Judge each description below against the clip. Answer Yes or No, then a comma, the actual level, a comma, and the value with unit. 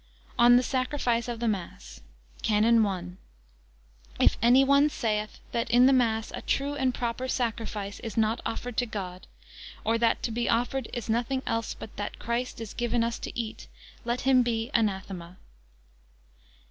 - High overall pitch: Yes, high, 235 Hz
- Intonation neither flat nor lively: No, narrow, 2.1 semitones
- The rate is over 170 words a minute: No, average, 165 wpm